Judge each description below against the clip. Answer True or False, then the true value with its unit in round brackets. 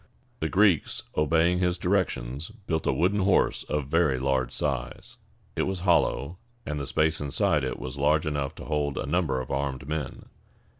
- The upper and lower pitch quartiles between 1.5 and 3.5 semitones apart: False (4.1 semitones)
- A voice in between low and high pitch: False (75 Hz)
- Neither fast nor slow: True (170 wpm)